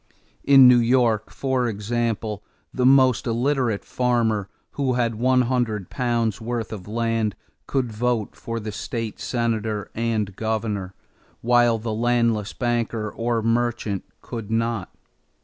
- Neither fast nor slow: No, slow, 125 wpm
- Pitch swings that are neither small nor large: No, narrow, 2.0 semitones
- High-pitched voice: No, low, 115 Hz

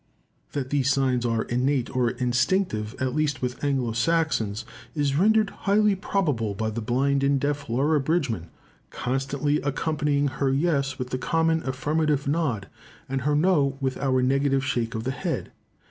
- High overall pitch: No, low, 135 Hz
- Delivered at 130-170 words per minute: Yes, average, 160 wpm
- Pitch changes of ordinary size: Yes, average, 3.0 semitones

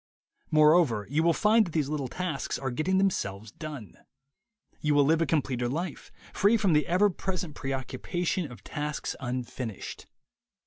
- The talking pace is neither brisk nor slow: Yes, average, 150 wpm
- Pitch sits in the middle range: Yes, medium, 150 Hz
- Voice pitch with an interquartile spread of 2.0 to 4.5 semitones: No, average, 5.0 semitones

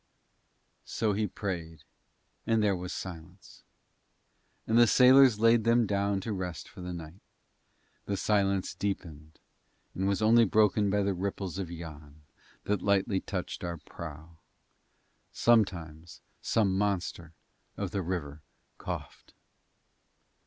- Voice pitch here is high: No, very low, 95 Hz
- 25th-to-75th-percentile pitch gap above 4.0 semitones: No, average, 3.5 semitones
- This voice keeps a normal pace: No, slow, 125 wpm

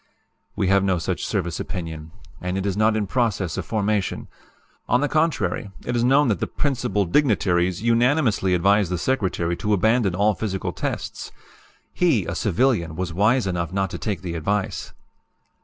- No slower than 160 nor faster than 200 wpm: Yes, average, 170 wpm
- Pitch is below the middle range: Yes, low, 100 Hz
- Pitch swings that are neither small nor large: Yes, average, 4.4 semitones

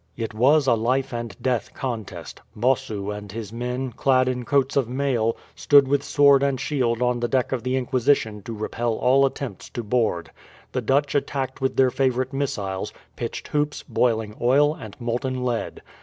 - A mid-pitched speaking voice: No, low, 125 Hz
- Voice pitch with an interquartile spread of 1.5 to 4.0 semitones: Yes, average, 2.8 semitones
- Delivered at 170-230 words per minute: Yes, average, 175 wpm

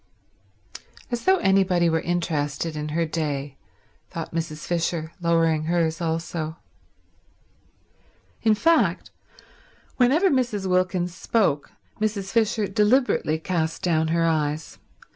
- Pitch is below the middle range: No, medium, 170 Hz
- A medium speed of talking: No, slow, 105 wpm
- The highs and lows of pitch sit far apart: No, average, 4.0 semitones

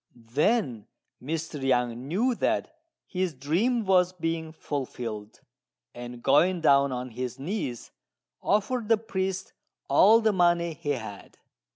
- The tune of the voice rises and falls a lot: Yes, wide, 7.1 semitones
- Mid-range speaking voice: Yes, medium, 160 Hz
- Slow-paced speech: Yes, slow, 120 wpm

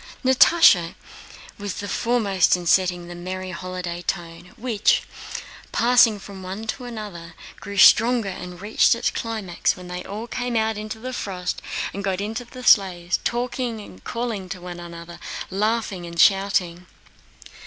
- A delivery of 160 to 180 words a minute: No, average, 145 wpm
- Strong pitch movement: No, average, 4.0 semitones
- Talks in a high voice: Yes, high, 195 Hz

